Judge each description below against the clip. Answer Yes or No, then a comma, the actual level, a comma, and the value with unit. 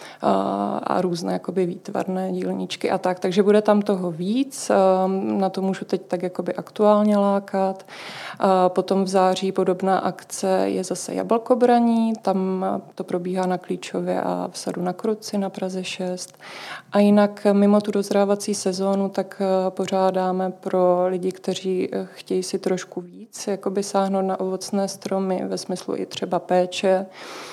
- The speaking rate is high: No, average, 145 wpm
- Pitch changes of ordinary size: No, narrow, 1.5 semitones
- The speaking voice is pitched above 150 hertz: Yes, high, 190 Hz